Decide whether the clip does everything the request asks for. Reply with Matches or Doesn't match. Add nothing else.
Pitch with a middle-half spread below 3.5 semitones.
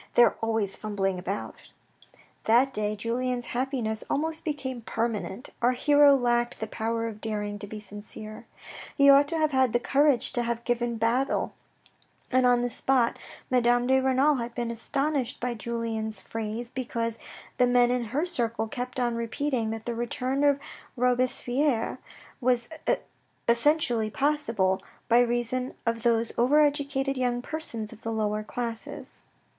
Matches